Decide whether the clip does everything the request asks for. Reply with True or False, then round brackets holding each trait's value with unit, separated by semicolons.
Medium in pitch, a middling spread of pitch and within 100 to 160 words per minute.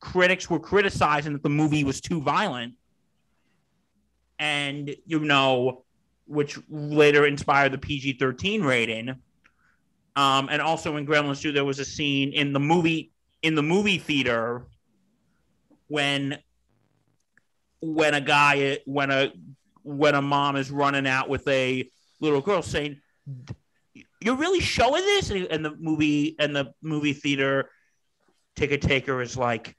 False (145 Hz; 2.1 semitones; 140 wpm)